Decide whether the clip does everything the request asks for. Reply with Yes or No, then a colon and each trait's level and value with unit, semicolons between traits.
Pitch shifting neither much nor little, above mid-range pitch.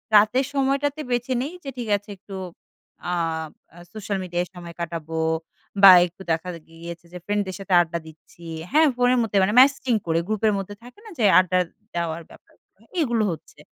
No: wide, 6.3 semitones; high, 200 Hz